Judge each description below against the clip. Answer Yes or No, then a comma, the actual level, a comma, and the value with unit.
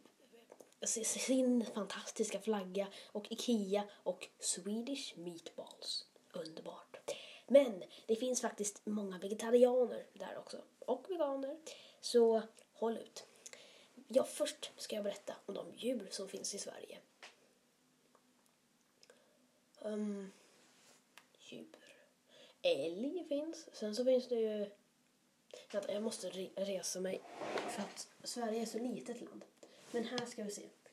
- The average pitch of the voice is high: Yes, high, 230 Hz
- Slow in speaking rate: Yes, slow, 115 wpm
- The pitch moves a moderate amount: Yes, average, 4.3 semitones